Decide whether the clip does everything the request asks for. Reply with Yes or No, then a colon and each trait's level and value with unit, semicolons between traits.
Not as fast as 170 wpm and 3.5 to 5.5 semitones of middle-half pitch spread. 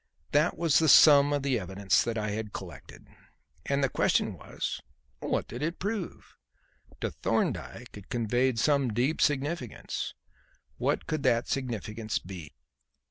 Yes: average, 140 wpm; average, 5.2 semitones